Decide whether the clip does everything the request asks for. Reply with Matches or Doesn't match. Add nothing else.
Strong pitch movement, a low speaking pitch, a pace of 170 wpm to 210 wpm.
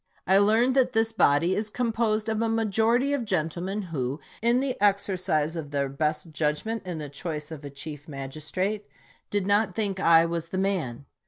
Doesn't match